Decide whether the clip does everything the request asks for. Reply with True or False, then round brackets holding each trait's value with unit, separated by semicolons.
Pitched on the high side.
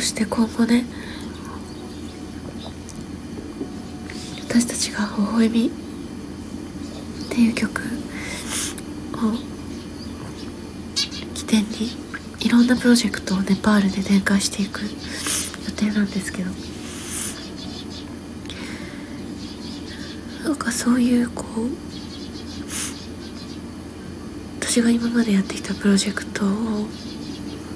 True (220 Hz)